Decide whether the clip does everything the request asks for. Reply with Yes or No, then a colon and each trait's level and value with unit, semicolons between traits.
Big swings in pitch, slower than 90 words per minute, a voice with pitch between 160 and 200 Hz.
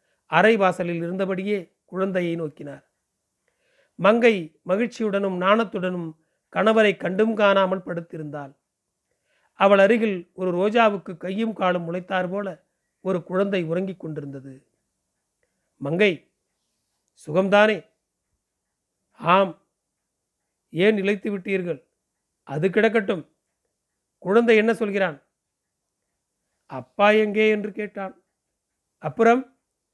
No: average, 3.4 semitones; average, 80 wpm; high, 195 Hz